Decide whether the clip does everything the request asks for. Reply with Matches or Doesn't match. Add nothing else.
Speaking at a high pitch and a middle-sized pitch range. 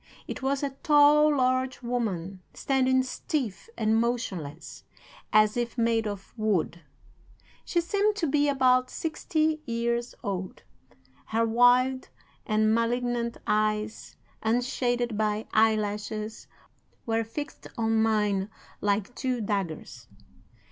Matches